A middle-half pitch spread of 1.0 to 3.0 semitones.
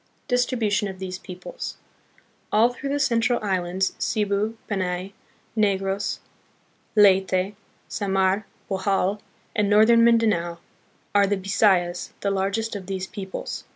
Yes: narrow, 2.4 semitones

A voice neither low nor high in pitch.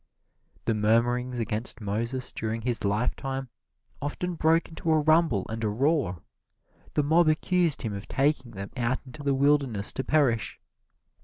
No: low, 130 Hz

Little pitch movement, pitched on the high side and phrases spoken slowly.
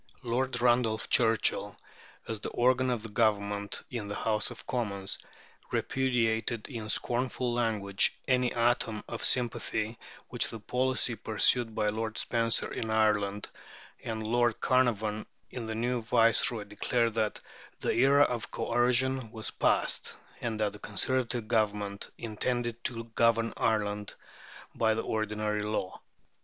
No: narrow, 2.2 semitones; low, 115 Hz; slow, 130 wpm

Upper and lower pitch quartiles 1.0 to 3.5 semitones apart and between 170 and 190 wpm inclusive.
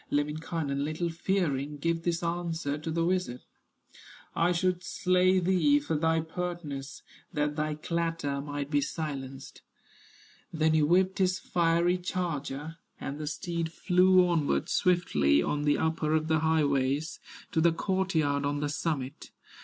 No: average, 3.0 semitones; average, 145 wpm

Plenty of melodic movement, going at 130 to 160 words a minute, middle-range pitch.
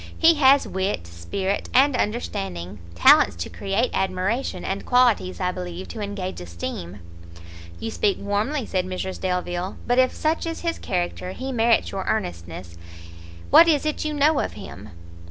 No: wide, 6.3 semitones; average, 155 wpm; high, 195 Hz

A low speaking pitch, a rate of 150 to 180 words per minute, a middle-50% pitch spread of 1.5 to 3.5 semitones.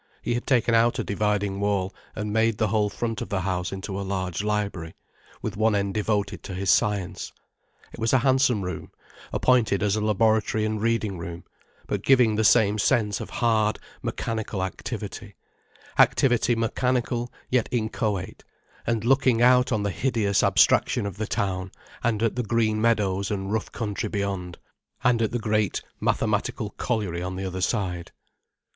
Yes: low, 105 Hz; average, 165 wpm; average, 2.7 semitones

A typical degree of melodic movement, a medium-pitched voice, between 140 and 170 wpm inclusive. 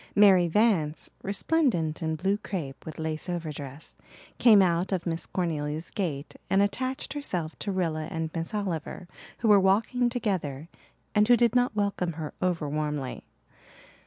Yes: average, 4.7 semitones; medium, 175 Hz; average, 150 wpm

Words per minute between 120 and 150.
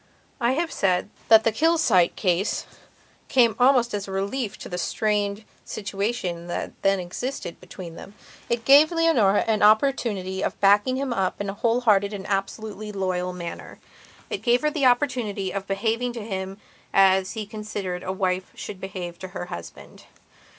No: average, 165 wpm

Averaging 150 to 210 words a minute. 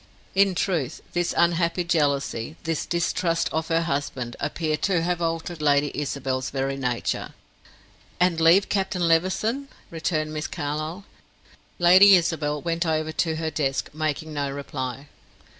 No: slow, 135 wpm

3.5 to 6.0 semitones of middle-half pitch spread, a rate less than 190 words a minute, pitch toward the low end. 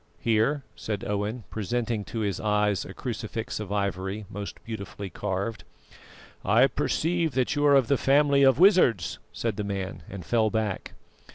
Yes: average, 3.9 semitones; average, 160 wpm; low, 110 Hz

